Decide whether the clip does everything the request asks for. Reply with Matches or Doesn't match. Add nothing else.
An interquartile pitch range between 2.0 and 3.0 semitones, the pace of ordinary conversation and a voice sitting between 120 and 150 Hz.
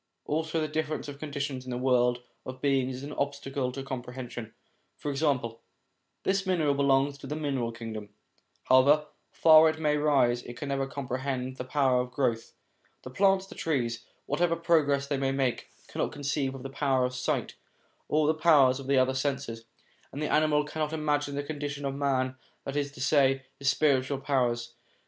Matches